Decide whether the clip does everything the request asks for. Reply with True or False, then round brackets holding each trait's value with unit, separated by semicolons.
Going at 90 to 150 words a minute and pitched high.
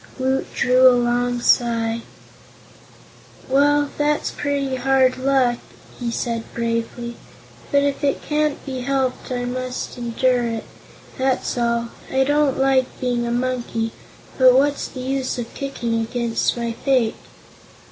True (135 wpm; 255 Hz)